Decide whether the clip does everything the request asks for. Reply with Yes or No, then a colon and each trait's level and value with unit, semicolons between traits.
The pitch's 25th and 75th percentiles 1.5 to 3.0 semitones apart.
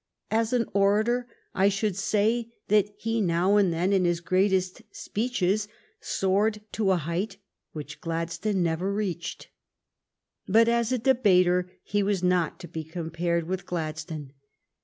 No: average, 3.7 semitones